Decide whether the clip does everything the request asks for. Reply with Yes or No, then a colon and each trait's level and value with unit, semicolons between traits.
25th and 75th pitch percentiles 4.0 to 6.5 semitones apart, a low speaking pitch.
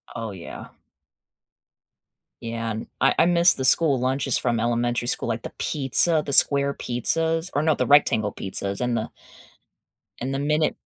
Yes: average, 4.4 semitones; low, 130 Hz